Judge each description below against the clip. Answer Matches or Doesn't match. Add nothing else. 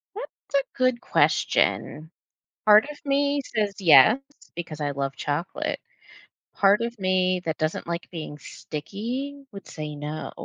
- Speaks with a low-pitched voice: Doesn't match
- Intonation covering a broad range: Matches